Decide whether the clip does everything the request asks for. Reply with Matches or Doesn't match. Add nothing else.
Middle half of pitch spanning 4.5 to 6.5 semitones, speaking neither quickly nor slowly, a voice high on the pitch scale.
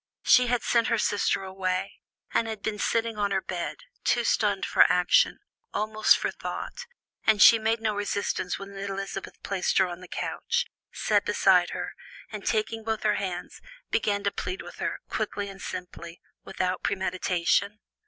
Doesn't match